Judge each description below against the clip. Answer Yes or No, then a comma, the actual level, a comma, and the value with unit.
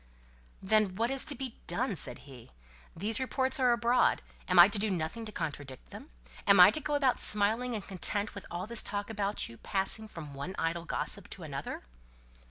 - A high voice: Yes, high, 205 Hz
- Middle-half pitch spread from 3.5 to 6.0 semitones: Yes, average, 4.9 semitones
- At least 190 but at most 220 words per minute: Yes, average, 195 wpm